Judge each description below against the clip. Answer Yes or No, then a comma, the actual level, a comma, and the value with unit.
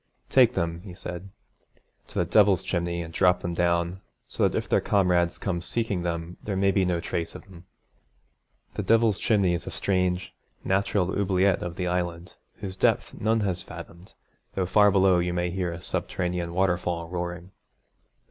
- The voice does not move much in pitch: Yes, narrow, 1.9 semitones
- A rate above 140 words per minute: Yes, average, 175 wpm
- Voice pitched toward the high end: No, very low, 90 Hz